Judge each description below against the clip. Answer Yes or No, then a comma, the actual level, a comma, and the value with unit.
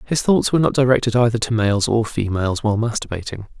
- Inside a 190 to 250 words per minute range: Yes, average, 200 wpm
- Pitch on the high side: No, low, 115 Hz